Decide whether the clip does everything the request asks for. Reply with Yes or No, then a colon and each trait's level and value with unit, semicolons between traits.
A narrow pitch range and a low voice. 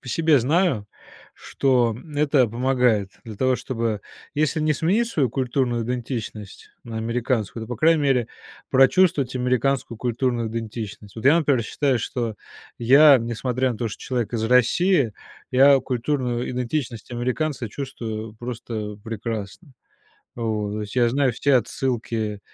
No: average, 3.2 semitones; low, 125 Hz